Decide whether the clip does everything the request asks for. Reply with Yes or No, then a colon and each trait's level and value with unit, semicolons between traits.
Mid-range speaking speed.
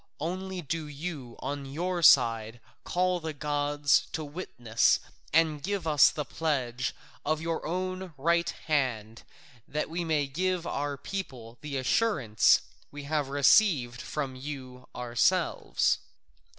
No: slow, 125 wpm